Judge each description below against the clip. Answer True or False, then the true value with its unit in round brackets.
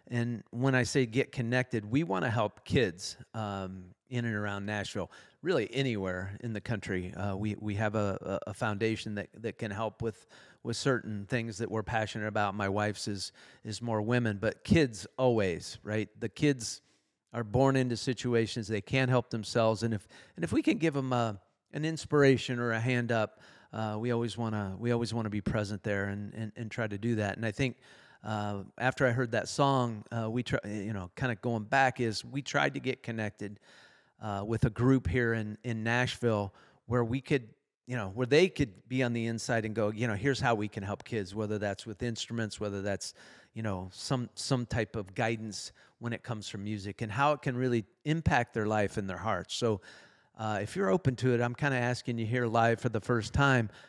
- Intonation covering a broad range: False (2.9 semitones)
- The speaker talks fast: True (215 wpm)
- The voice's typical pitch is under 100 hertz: False (115 Hz)